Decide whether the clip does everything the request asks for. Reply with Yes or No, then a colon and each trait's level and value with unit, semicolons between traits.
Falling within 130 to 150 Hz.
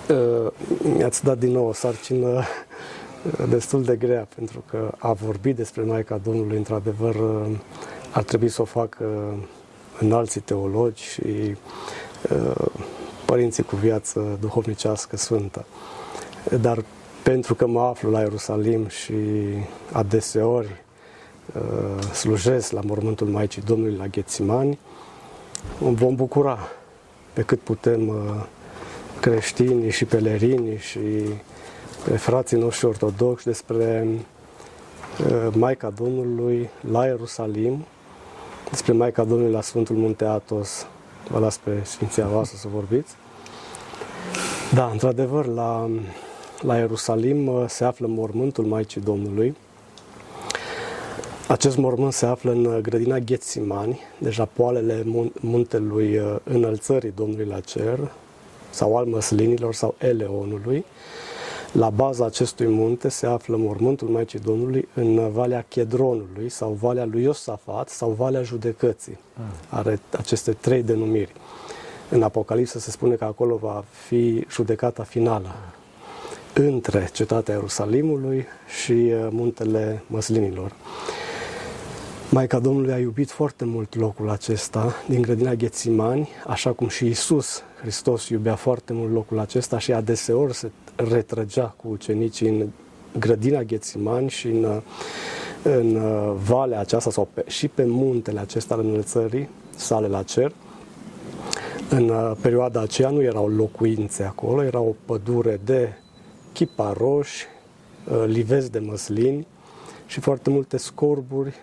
No: low, 115 Hz